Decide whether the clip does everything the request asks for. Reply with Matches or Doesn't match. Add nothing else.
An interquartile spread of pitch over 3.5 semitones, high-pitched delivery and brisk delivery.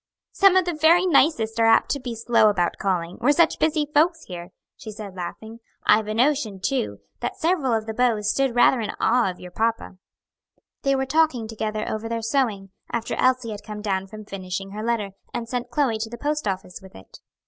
Matches